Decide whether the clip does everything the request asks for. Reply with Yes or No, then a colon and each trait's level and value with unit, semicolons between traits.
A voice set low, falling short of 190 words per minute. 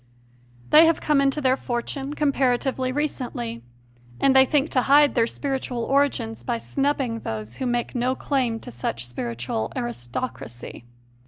No: very high, 255 Hz; average, 145 wpm